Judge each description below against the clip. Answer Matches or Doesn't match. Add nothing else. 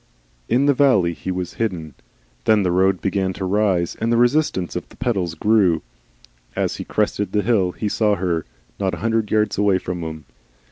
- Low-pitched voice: Matches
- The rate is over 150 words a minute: Matches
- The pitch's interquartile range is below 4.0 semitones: Matches